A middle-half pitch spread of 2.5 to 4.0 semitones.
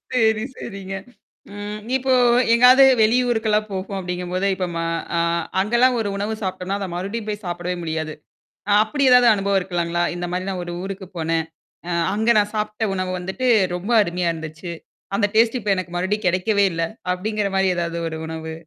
Yes: average, 3.4 semitones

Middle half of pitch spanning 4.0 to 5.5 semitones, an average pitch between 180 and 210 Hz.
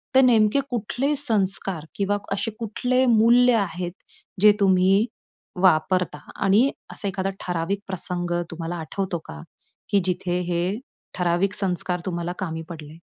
No: average, 3.3 semitones; high, 190 Hz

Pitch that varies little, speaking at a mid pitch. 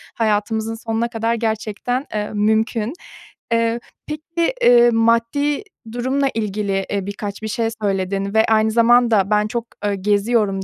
No: narrow, 2.2 semitones; high, 225 Hz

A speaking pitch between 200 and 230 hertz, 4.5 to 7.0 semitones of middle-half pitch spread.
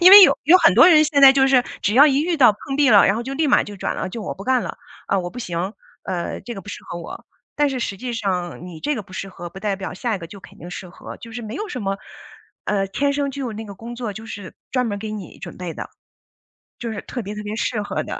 Yes: high, 220 Hz; wide, 5.4 semitones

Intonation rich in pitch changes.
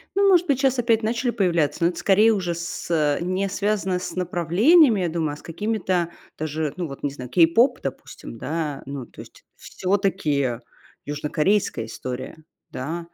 Yes: wide, 5.9 semitones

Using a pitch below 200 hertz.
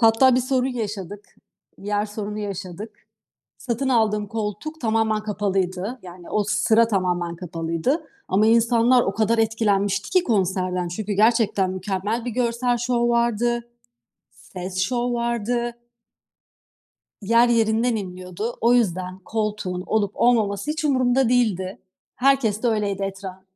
No: high, 215 Hz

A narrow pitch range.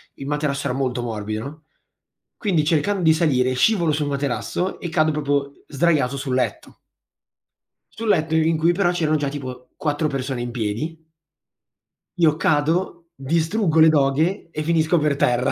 No: average, 3.2 semitones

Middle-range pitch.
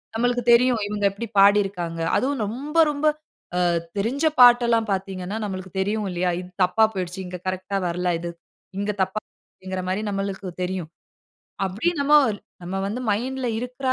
No: high, 200 Hz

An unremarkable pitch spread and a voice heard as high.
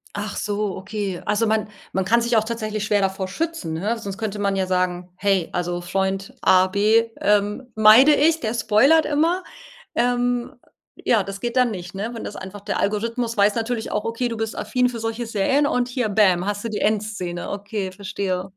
Yes: average, 3.2 semitones; high, 210 Hz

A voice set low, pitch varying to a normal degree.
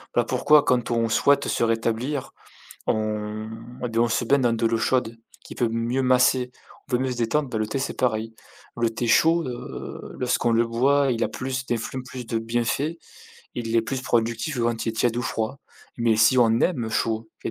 No: low, 120 Hz; narrow, 2.2 semitones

